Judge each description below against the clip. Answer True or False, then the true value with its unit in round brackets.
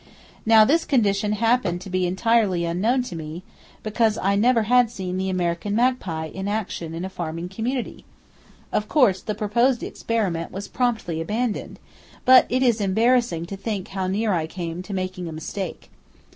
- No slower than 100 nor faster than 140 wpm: False (170 wpm)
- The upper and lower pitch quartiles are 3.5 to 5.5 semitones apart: True (4.3 semitones)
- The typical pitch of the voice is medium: False (200 Hz)